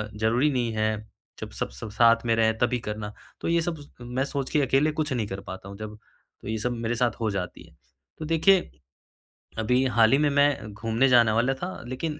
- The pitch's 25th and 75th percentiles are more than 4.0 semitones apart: Yes, average, 4.4 semitones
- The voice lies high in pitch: No, low, 120 Hz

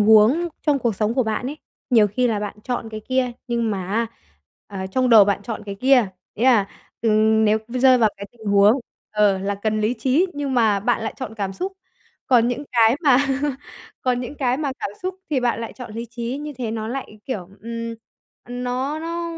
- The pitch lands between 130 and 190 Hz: No, high, 235 Hz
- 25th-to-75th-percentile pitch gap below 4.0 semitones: Yes, average, 3.4 semitones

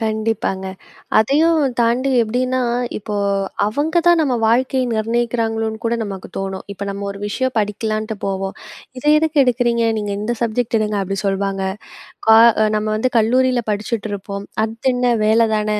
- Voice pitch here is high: Yes, high, 225 Hz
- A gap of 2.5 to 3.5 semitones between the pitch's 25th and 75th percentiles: Yes, average, 3.1 semitones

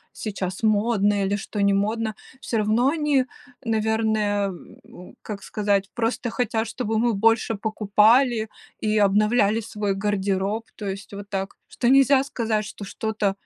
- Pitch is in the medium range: No, high, 215 Hz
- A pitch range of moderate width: No, narrow, 2.0 semitones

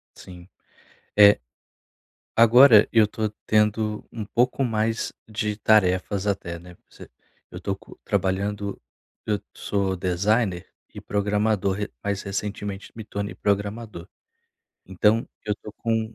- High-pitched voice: No, low, 105 Hz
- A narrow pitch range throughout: Yes, narrow, 1.8 semitones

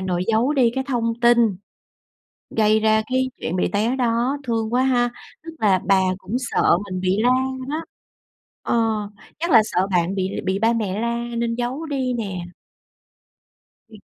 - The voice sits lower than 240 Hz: Yes, high, 230 Hz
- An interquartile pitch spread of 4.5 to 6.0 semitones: No, average, 3.9 semitones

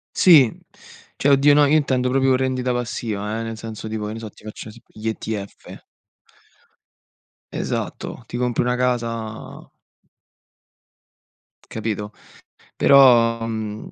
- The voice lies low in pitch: Yes, low, 115 Hz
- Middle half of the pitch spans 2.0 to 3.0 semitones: Yes, average, 2.7 semitones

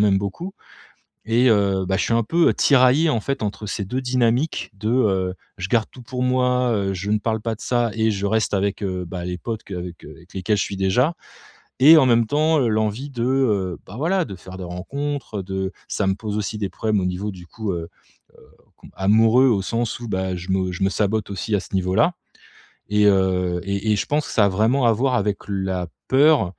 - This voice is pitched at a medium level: No, low, 105 Hz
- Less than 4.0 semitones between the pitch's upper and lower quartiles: No, average, 4.5 semitones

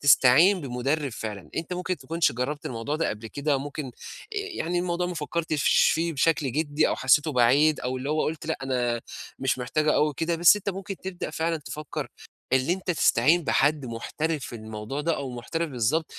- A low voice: No, medium, 150 Hz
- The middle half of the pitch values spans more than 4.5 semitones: No, average, 4.2 semitones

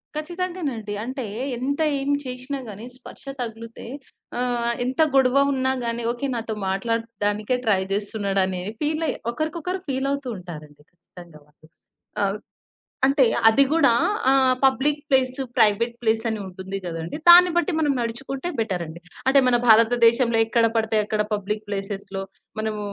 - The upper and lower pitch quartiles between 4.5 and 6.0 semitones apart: Yes, average, 4.8 semitones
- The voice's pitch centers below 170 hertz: No, high, 230 Hz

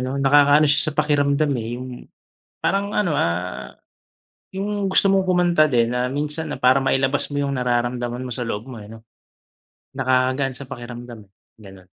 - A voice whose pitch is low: Yes, low, 130 Hz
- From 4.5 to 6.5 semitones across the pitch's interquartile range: No, average, 3.5 semitones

